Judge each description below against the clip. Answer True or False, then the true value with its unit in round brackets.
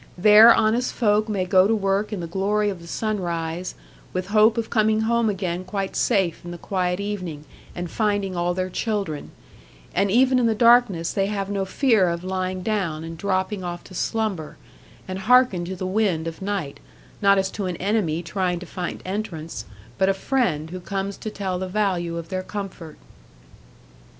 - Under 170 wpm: False (185 wpm)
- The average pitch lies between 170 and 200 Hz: True (190 Hz)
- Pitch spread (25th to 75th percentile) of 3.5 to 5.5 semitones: False (3.1 semitones)